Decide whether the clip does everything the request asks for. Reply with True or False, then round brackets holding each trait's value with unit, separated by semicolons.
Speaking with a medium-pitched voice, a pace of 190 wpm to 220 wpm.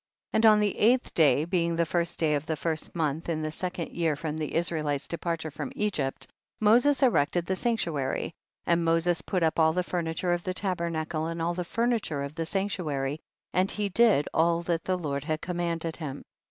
True (170 Hz; 205 wpm)